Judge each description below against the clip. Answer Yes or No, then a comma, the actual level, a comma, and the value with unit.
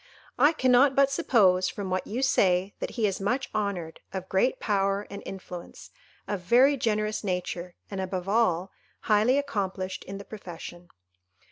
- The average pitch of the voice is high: Yes, high, 200 Hz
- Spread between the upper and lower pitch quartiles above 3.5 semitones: Yes, average, 4.2 semitones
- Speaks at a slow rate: No, average, 155 wpm